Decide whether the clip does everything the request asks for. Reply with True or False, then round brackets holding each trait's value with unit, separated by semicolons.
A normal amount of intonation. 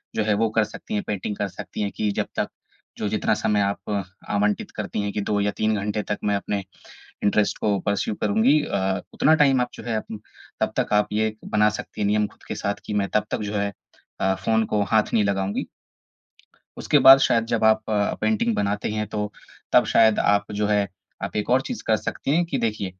False (1.3 semitones)